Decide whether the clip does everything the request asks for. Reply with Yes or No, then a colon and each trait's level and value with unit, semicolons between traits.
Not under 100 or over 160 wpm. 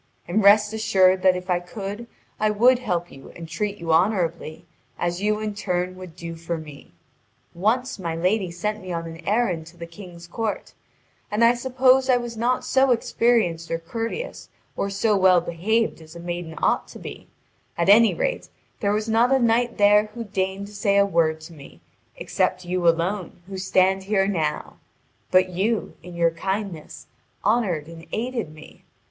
No: average, 180 wpm